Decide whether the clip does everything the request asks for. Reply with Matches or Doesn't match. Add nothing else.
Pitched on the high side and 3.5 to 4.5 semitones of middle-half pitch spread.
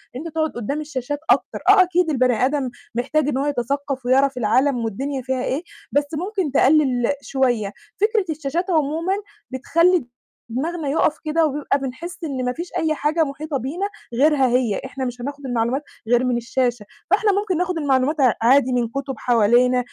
Matches